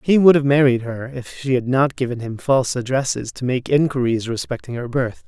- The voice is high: No, low, 130 Hz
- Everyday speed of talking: No, fast, 215 wpm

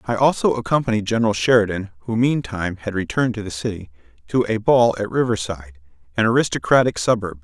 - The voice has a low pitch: Yes, low, 105 Hz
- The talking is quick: No, slow, 135 wpm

